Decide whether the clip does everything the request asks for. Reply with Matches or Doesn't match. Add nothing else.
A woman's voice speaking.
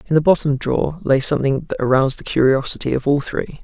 Doesn't match